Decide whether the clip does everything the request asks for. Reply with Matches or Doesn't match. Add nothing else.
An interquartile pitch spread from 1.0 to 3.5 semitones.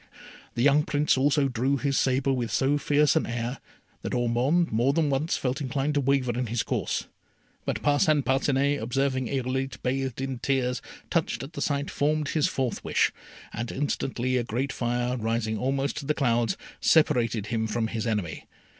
Matches